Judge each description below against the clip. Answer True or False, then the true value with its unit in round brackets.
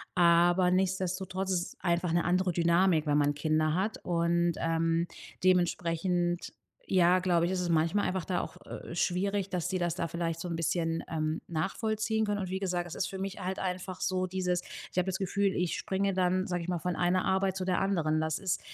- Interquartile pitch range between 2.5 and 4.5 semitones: False (1.9 semitones)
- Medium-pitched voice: True (180 Hz)